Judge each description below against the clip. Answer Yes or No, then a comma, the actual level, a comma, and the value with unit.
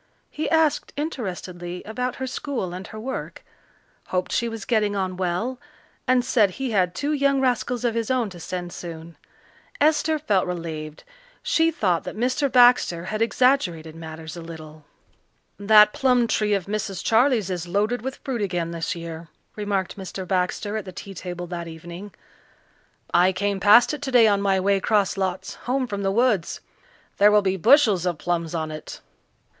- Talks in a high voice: Yes, high, 200 Hz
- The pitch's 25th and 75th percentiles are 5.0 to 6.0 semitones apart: Yes, wide, 5.6 semitones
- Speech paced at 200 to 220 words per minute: No, average, 170 wpm